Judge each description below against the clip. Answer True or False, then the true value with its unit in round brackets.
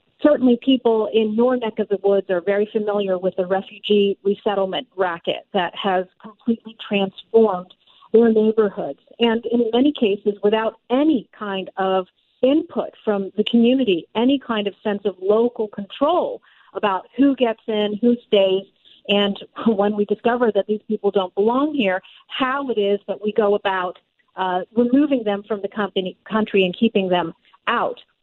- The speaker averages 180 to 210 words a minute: False (160 wpm)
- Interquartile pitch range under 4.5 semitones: True (2.9 semitones)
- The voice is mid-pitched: False (210 Hz)